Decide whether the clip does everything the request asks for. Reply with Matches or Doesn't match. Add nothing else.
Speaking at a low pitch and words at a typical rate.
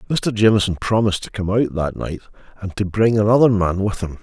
Doesn't match